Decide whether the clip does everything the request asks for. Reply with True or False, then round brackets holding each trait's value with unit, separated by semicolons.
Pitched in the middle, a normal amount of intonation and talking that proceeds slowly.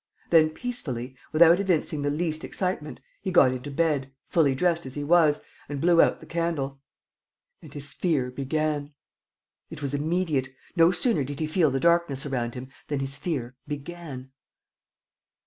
False (150 Hz; 3.7 semitones; 160 wpm)